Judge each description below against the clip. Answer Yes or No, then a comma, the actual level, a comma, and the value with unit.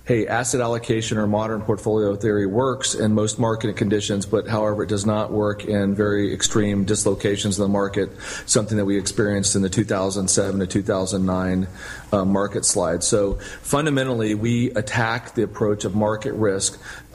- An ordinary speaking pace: Yes, average, 160 wpm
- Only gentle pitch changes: Yes, narrow, 1.9 semitones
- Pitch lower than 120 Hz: Yes, low, 105 Hz